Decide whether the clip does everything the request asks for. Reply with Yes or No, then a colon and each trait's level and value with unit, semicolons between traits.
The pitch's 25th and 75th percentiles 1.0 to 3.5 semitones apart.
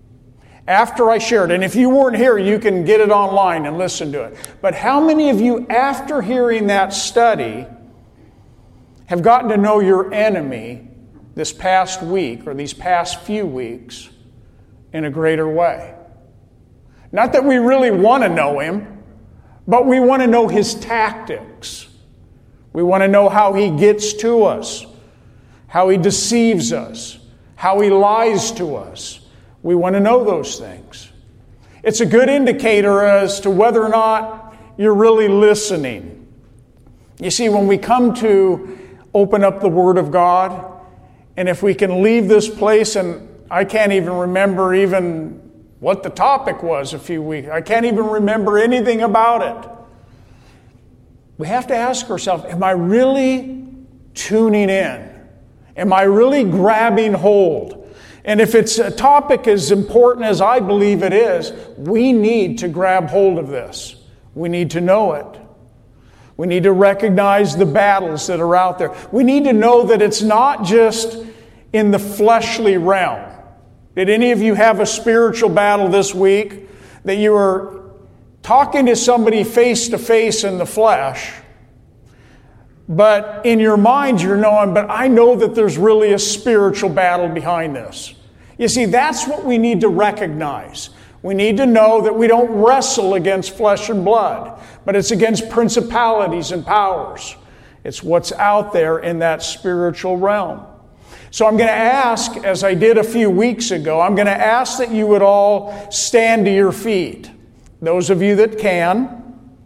No: average, 4.1 semitones